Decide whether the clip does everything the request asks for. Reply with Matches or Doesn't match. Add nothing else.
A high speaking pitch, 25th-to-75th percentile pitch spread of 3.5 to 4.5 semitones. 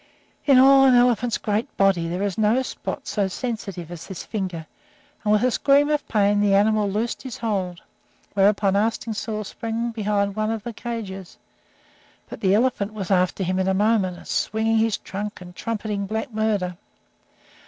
Doesn't match